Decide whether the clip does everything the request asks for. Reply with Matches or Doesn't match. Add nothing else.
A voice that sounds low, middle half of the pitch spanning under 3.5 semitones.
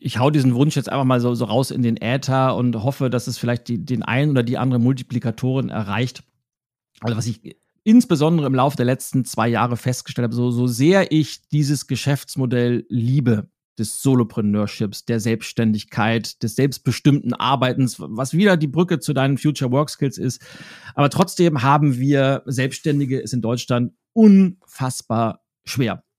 Matches